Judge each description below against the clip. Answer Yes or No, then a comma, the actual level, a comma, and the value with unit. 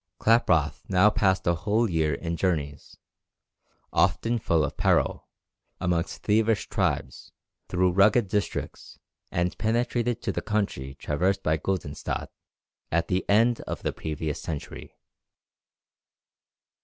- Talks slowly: Yes, slow, 120 wpm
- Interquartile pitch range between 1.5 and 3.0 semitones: No, average, 4.8 semitones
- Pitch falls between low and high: No, very low, 95 Hz